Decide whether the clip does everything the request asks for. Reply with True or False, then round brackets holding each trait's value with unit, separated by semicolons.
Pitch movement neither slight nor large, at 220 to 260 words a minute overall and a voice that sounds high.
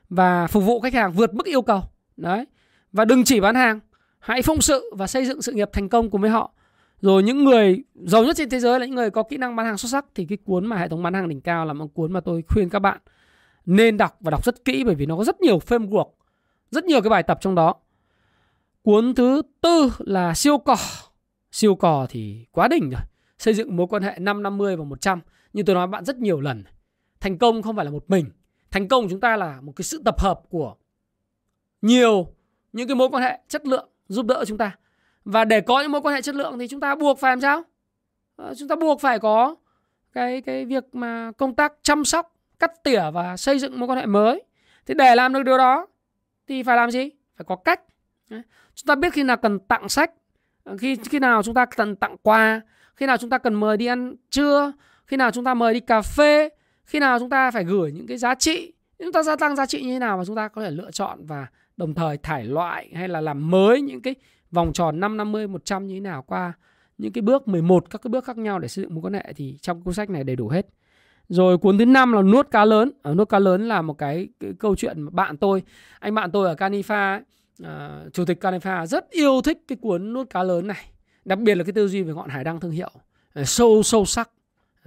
False (6.0 semitones; 250 wpm; 220 Hz)